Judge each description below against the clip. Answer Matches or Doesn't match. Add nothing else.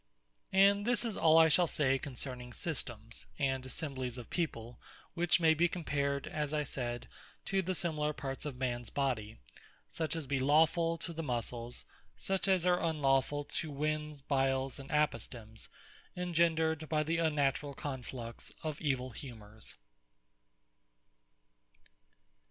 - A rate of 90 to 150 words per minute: Matches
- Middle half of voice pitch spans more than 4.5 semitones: Doesn't match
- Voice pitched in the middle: Matches